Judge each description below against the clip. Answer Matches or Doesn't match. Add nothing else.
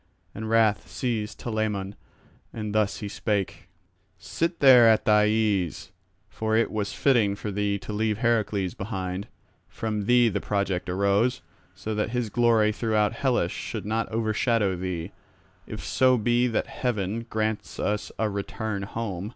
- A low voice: Matches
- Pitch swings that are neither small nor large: Doesn't match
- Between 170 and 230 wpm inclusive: Doesn't match